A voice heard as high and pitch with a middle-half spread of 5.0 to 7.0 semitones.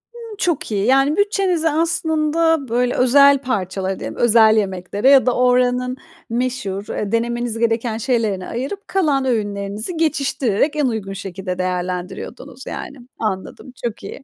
Yes: high, 245 Hz; wide, 5.5 semitones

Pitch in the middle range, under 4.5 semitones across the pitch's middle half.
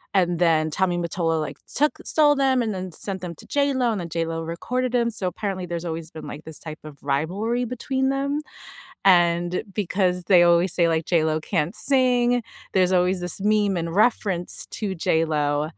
No: medium, 180 Hz; average, 5.2 semitones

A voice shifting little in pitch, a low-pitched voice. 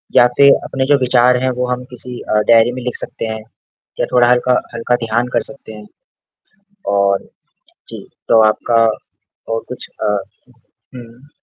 Yes: narrow, 1.8 semitones; low, 120 Hz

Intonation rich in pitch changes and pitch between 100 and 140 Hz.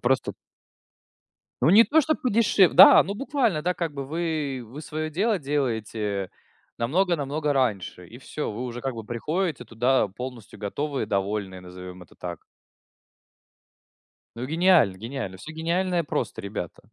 Yes: wide, 7.5 semitones; low, 135 Hz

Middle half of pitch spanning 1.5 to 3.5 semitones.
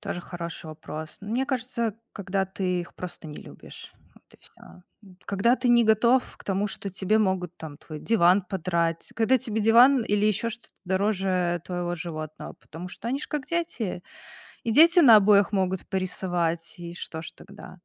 No: average, 4.3 semitones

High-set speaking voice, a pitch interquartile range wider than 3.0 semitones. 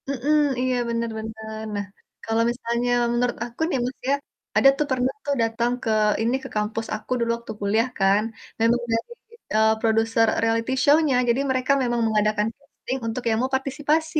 No: high, 235 Hz; average, 2.7 semitones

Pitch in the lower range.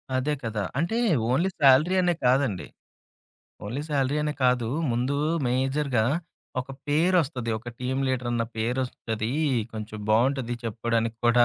Yes: low, 125 Hz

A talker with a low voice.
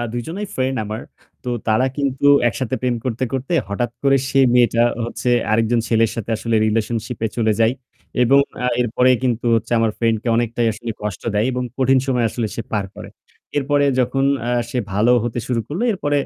Yes: low, 120 Hz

